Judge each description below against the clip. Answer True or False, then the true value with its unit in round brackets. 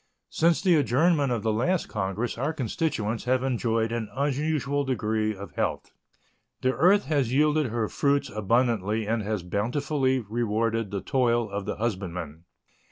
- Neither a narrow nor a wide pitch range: True (4.7 semitones)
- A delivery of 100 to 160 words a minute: True (150 wpm)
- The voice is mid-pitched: False (120 Hz)